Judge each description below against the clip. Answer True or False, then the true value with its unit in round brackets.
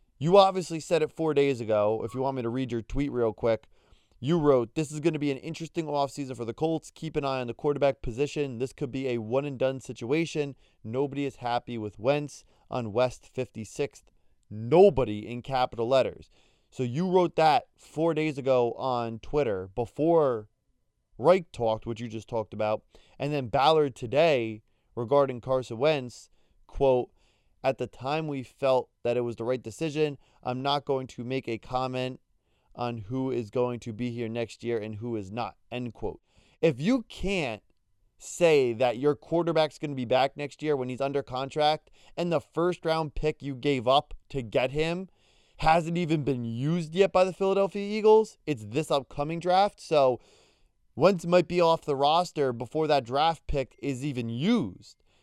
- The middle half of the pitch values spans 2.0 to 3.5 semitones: False (4.4 semitones)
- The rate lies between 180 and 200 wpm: True (185 wpm)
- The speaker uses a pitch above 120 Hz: True (135 Hz)